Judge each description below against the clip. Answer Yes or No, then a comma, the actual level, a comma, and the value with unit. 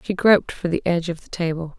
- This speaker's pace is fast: Yes, fast, 270 wpm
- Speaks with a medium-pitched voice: Yes, medium, 175 Hz